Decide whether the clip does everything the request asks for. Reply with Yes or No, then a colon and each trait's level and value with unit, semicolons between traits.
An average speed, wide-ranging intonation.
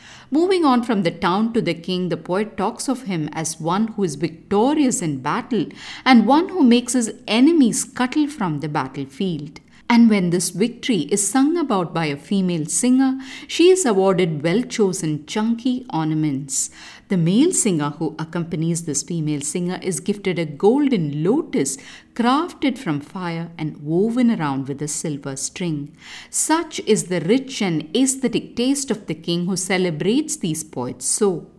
Yes: average, 165 wpm; wide, 7.1 semitones